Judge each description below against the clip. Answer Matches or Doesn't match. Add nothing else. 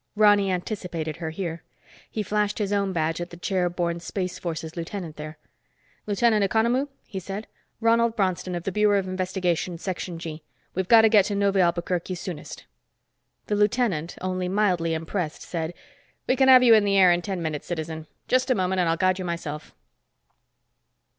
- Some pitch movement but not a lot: Matches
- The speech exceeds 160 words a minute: Matches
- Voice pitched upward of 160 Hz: Matches